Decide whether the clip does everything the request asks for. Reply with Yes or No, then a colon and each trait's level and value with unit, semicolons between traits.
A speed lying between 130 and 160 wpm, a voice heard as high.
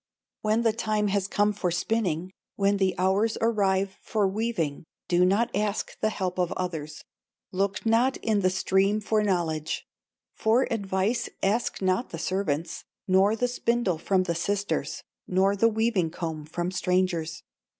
Yes: average, 150 wpm; high, 195 Hz